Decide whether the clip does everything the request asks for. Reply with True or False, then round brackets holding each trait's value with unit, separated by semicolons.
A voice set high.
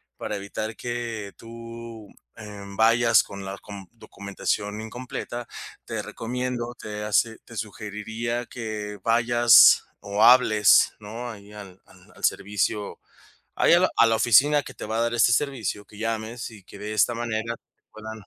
False (110 Hz)